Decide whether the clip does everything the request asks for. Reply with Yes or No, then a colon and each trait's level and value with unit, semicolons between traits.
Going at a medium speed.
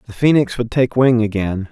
No: fast, 210 wpm